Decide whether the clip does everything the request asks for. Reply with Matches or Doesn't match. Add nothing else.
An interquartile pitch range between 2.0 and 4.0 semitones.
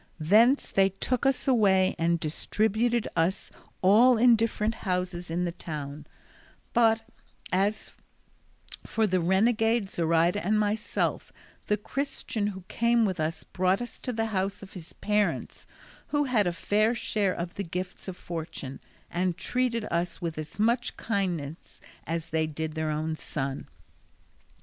Doesn't match